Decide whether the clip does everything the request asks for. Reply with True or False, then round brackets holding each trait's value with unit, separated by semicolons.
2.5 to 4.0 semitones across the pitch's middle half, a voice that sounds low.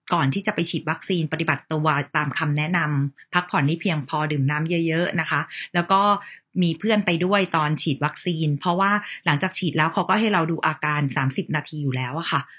False (3.3 semitones; 160 Hz)